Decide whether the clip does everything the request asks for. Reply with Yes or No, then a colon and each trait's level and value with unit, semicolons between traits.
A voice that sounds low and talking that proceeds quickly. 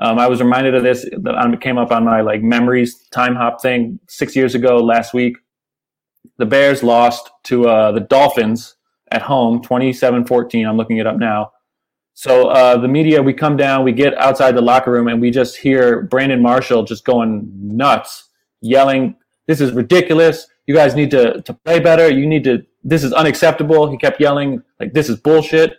No: low, 125 Hz; average, 195 wpm